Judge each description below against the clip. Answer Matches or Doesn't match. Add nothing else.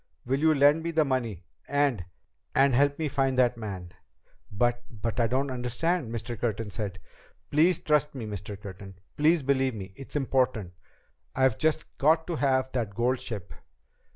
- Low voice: Matches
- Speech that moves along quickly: Doesn't match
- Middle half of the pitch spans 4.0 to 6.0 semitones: Matches